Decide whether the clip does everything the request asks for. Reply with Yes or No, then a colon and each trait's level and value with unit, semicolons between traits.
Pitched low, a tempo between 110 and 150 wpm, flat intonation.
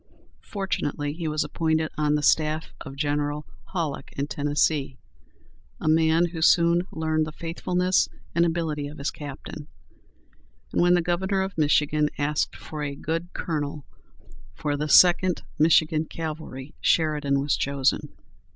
No: medium, 155 Hz; average, 140 wpm; narrow, 2.2 semitones